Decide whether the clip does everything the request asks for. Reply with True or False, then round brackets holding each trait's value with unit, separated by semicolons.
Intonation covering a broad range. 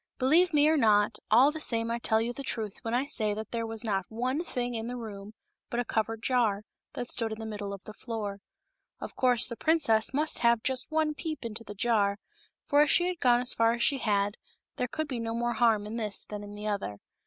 False (3.1 semitones)